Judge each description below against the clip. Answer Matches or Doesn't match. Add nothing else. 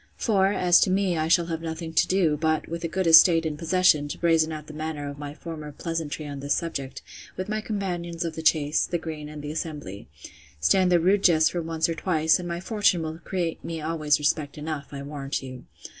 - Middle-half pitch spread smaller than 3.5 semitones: Matches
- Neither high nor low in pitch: Matches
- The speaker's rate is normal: Doesn't match